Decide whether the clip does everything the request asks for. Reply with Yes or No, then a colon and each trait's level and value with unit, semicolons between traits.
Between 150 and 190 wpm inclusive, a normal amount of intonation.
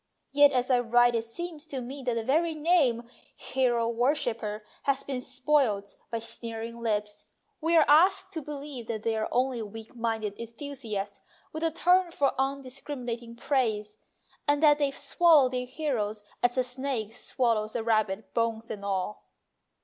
Yes: average, 170 wpm; average, 4.2 semitones